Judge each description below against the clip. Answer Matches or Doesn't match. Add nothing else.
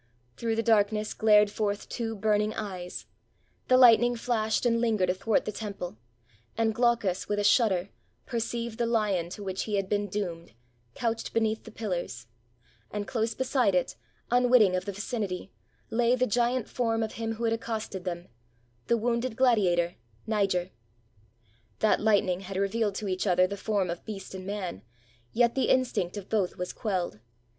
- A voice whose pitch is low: Doesn't match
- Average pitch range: Matches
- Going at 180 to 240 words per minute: Doesn't match